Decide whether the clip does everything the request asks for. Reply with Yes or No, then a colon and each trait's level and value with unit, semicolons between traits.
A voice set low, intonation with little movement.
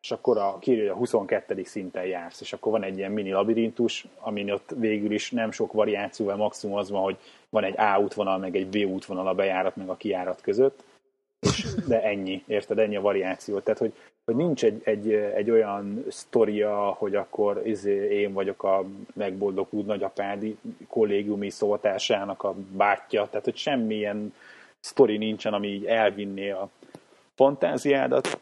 Yes: low, 105 Hz; narrow, 1.6 semitones